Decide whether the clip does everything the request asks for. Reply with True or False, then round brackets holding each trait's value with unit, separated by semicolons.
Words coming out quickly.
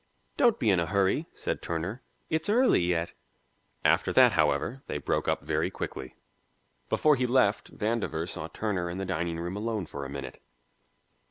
False (170 wpm)